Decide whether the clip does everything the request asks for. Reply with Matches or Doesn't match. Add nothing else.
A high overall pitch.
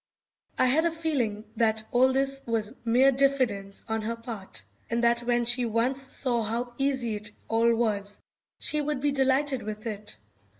Matches